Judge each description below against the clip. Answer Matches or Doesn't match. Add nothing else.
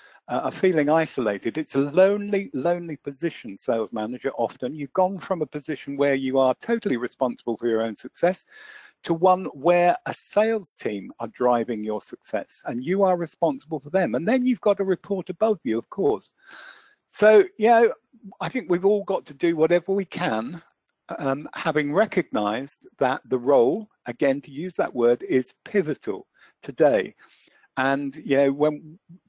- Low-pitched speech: Doesn't match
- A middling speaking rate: Matches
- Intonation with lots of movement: Matches